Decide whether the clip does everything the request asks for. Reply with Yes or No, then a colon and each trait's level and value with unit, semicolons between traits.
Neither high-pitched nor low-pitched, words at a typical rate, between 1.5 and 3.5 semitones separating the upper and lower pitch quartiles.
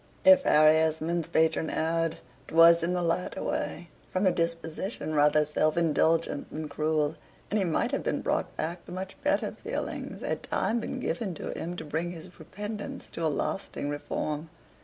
Yes: medium, 165 Hz; average, 175 wpm; narrow, 2.4 semitones